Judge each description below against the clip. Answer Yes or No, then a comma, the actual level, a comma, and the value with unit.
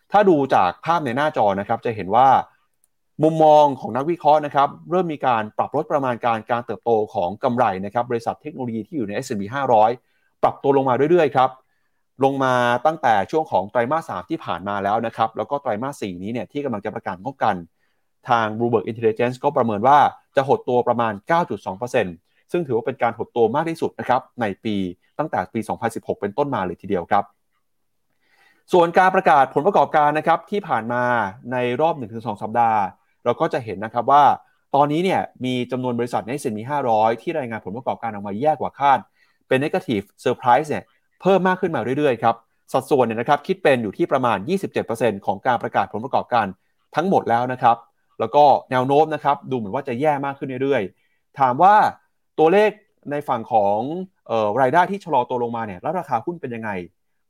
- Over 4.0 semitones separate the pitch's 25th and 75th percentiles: Yes, average, 5.2 semitones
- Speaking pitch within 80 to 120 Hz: No, low, 130 Hz